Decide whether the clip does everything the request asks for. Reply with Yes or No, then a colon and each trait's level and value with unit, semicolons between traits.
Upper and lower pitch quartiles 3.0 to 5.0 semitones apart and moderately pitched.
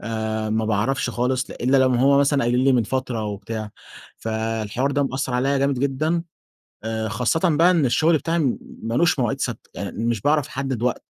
No: average, 3.7 semitones; low, 125 Hz